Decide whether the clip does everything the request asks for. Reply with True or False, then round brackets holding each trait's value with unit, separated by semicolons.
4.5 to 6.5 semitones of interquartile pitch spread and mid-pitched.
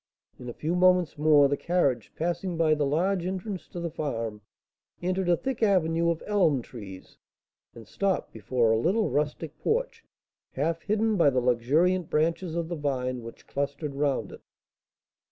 True (4.8 semitones; 160 Hz)